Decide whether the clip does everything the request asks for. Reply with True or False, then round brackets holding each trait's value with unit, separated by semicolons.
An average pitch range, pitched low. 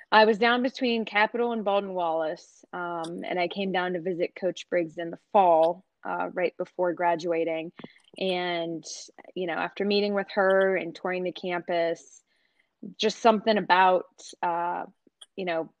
False (3.0 semitones; 180 Hz)